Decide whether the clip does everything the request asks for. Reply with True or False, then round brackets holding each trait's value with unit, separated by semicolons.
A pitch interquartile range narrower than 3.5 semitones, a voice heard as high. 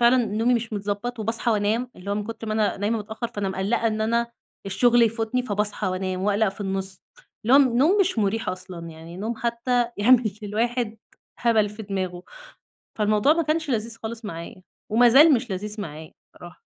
True (3.0 semitones; 220 Hz)